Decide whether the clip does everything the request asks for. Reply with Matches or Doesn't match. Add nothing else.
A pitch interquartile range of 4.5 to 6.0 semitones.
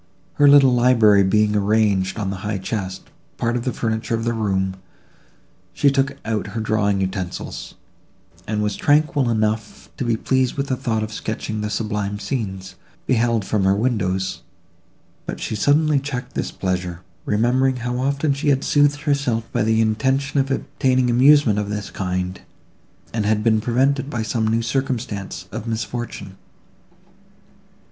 Doesn't match